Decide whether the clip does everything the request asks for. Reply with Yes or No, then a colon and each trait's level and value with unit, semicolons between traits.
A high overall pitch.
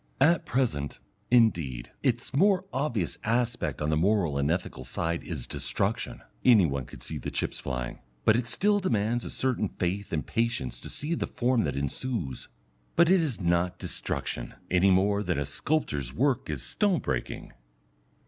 No: low, 100 Hz